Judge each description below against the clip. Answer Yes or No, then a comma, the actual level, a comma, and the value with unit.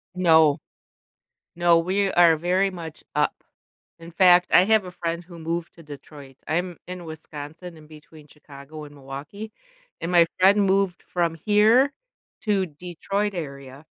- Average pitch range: Yes, average, 3.3 semitones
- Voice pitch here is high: No, medium, 170 Hz